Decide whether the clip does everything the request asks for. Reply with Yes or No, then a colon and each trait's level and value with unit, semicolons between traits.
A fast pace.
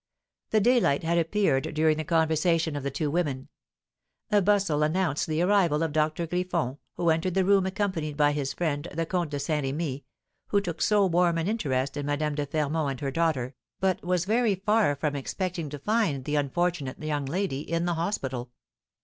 No: average, 190 wpm